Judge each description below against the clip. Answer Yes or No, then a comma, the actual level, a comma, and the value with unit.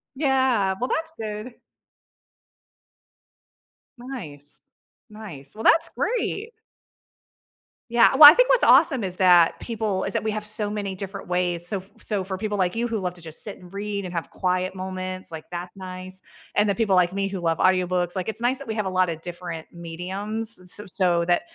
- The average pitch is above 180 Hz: Yes, high, 190 Hz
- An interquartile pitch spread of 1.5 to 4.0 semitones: Yes, average, 3.4 semitones